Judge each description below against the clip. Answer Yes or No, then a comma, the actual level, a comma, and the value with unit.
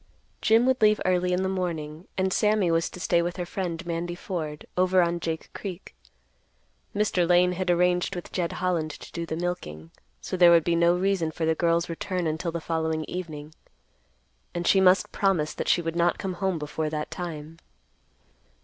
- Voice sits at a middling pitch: Yes, medium, 175 Hz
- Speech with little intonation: Yes, narrow, 2.1 semitones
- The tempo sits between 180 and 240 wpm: Yes, average, 190 wpm